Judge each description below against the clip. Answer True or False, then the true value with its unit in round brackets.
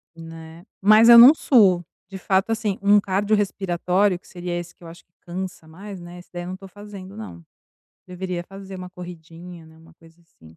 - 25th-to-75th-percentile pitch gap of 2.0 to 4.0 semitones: True (2.4 semitones)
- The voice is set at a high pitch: False (180 Hz)